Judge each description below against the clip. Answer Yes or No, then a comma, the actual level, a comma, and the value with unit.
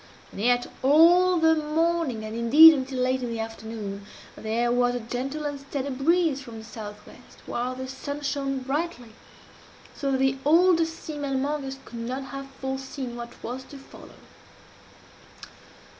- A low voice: No, very high, 265 Hz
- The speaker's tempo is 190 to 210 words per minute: No, average, 160 wpm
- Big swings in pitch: No, average, 3.5 semitones